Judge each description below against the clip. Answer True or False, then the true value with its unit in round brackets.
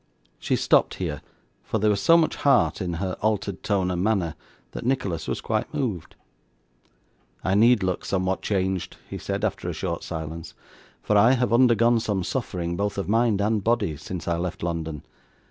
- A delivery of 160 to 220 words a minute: True (180 wpm)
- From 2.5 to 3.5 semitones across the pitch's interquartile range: False (4.2 semitones)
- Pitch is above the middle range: False (100 Hz)